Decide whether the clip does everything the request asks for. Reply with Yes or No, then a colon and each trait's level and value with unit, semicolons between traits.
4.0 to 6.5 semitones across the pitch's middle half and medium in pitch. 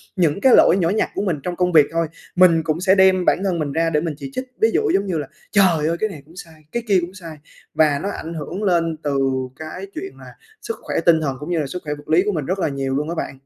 No: average, 3.5 semitones; medium, 170 Hz